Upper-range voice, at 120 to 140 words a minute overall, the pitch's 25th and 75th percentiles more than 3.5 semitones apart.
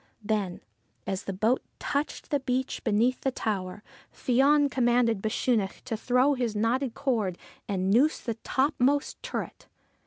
Yes: high, 240 Hz; slow, 135 wpm; average, 4.0 semitones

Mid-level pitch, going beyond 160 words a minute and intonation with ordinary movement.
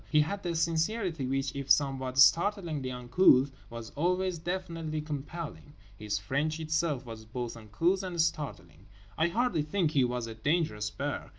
No: medium, 150 Hz; average, 155 wpm; average, 4.9 semitones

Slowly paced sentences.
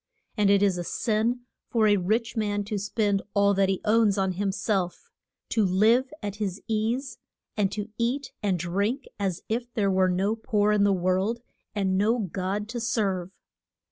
No: average, 180 wpm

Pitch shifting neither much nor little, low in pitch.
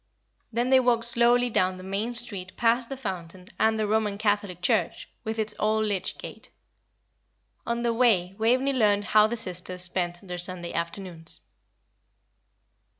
No: average, 4.2 semitones; high, 210 Hz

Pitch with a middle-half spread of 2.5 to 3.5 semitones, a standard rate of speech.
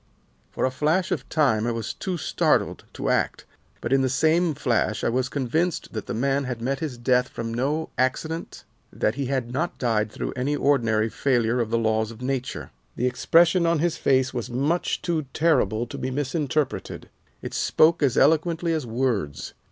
No: average, 4.7 semitones; average, 185 wpm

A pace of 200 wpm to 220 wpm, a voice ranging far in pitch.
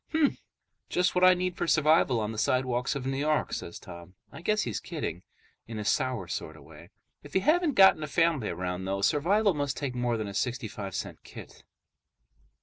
Yes: fast, 205 wpm; wide, 8.5 semitones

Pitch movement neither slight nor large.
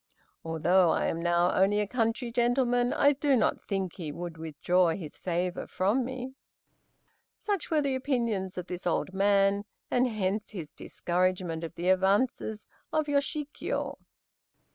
No: wide, 5.9 semitones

